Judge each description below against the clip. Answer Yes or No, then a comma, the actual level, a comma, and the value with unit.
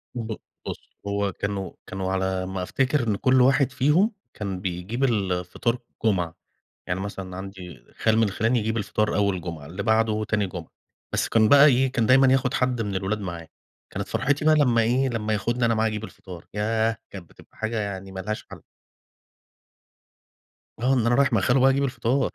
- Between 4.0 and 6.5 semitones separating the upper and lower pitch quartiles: Yes, average, 4.7 semitones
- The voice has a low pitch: Yes, low, 110 Hz